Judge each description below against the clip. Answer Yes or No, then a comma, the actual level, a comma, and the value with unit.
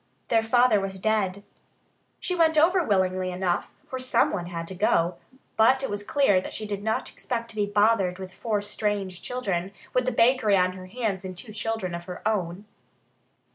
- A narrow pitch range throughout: No, average, 3.7 semitones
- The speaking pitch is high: Yes, high, 205 Hz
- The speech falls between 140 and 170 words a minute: No, average, 185 wpm